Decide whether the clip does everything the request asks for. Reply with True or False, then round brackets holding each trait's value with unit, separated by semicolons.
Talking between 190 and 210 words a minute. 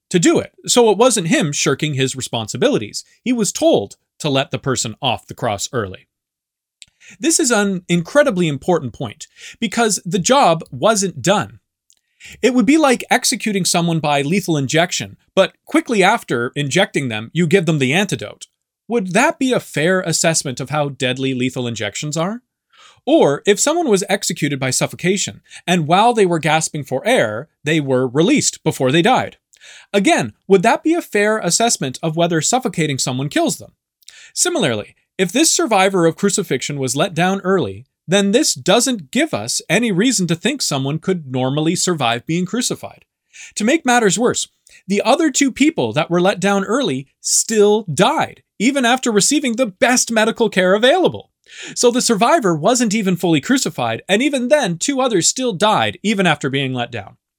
False (170 wpm)